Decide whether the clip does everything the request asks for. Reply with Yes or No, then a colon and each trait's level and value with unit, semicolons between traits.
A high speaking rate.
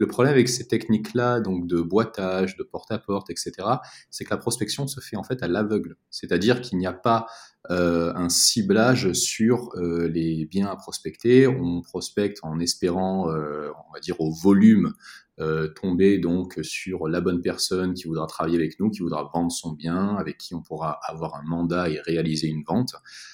No: average, 195 wpm